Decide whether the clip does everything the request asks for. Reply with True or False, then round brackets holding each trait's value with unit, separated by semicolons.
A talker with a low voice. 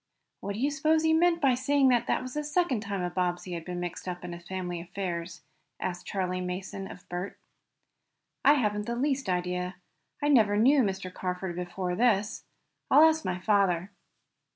False (195 Hz)